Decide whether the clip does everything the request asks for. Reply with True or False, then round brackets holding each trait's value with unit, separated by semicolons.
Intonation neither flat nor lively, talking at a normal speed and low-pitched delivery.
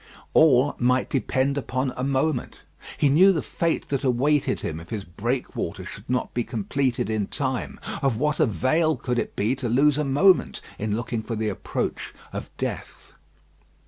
True (3.4 semitones; 170 wpm; 130 Hz)